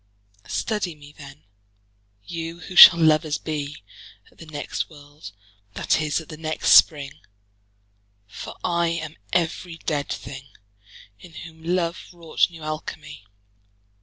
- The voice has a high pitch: No, medium, 155 Hz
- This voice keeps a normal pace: No, slow, 130 wpm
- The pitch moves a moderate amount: No, narrow, 2.3 semitones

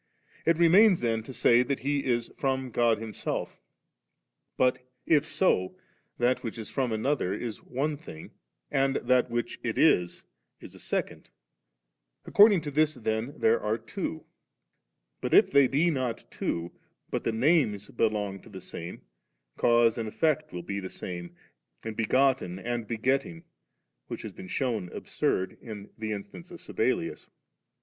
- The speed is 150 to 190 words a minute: Yes, average, 155 wpm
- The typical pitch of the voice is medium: No, low, 120 Hz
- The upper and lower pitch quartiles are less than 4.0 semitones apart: No, average, 4.6 semitones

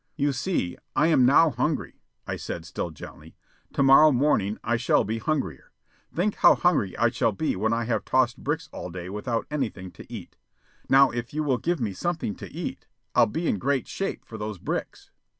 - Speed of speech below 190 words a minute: No, average, 200 wpm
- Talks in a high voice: No, low, 125 Hz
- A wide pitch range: Yes, wide, 6.3 semitones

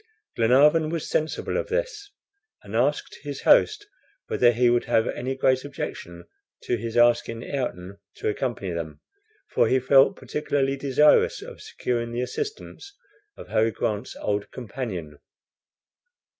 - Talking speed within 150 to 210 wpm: No, slow, 135 wpm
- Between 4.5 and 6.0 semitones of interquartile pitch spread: No, average, 4.1 semitones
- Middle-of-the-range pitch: No, low, 125 Hz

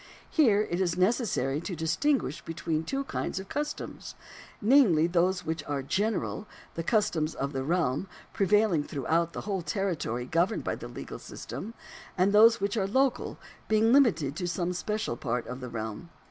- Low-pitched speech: No, medium, 180 Hz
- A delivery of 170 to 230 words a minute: Yes, average, 175 wpm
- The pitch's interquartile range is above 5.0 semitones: Yes, wide, 5.5 semitones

